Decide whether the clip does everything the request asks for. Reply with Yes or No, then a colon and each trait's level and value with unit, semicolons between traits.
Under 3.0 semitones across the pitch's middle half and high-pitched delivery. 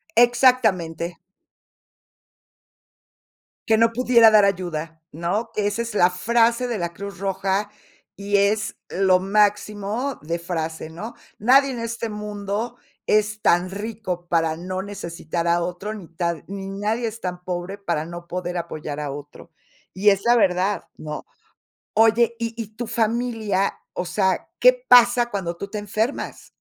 No: average, 4.3 semitones; high, 200 Hz